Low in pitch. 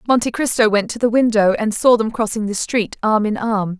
No: high, 220 Hz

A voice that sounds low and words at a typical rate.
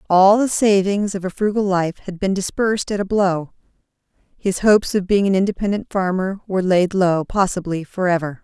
No: high, 190 Hz; average, 180 wpm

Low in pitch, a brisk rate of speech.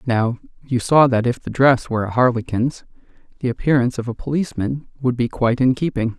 No: low, 125 Hz; average, 195 wpm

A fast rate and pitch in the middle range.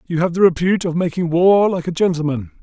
Yes: fast, 230 wpm; medium, 170 Hz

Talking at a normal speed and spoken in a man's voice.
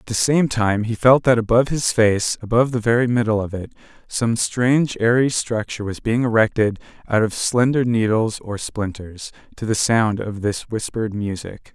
Yes: average, 185 wpm; male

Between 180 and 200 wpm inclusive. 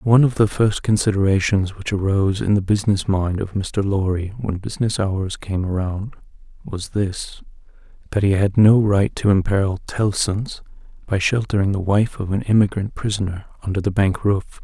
No: average, 165 wpm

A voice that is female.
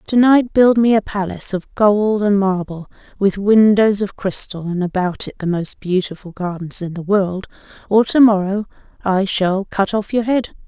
Yes: female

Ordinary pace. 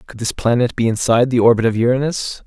No: fast, 220 wpm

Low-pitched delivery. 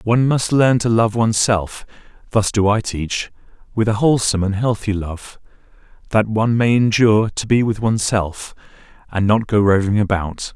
Yes: low, 110 Hz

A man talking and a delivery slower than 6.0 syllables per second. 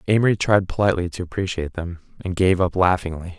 No: male; 6.6 syllables/s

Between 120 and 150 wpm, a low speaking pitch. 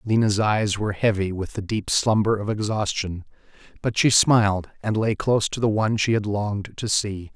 No: average, 195 wpm; low, 105 Hz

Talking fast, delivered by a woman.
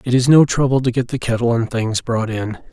No: fast, 265 wpm; male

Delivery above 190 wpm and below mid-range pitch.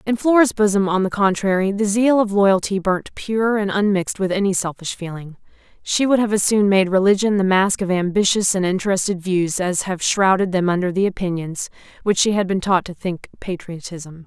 No: average, 200 wpm; high, 195 Hz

